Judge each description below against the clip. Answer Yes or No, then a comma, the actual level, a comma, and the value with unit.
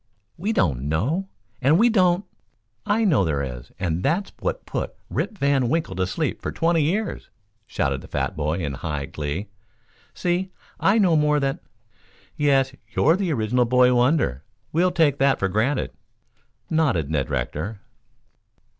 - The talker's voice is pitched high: No, low, 130 Hz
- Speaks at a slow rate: No, average, 160 wpm